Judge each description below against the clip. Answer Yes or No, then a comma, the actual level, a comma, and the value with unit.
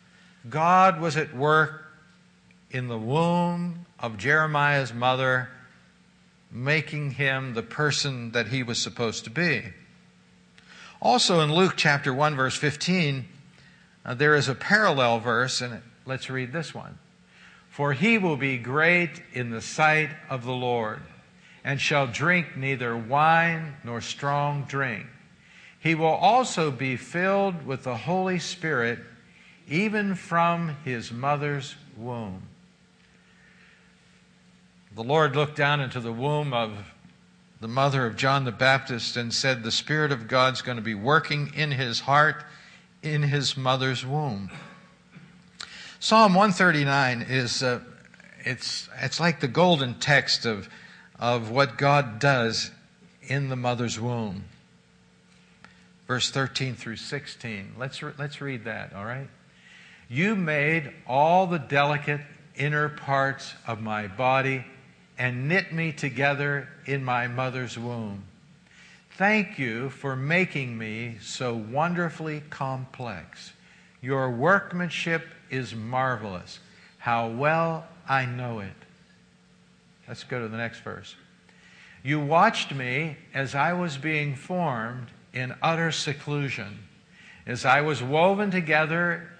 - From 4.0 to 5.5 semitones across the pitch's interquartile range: Yes, average, 4.4 semitones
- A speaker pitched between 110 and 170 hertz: Yes, medium, 140 Hz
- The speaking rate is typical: No, slow, 125 wpm